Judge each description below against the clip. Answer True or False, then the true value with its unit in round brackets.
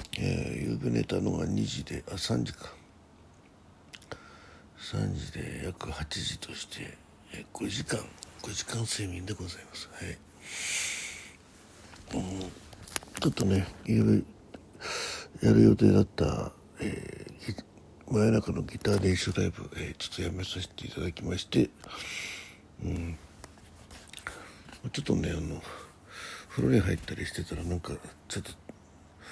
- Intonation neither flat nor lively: True (3.0 semitones)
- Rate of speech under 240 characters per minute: True (225 characters per minute)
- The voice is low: True (90 Hz)